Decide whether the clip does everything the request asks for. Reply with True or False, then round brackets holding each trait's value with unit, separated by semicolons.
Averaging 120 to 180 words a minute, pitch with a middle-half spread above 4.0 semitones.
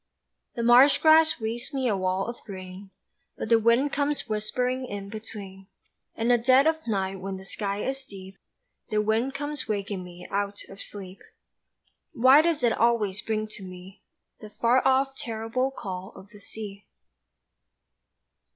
True (160 wpm; 4.6 semitones)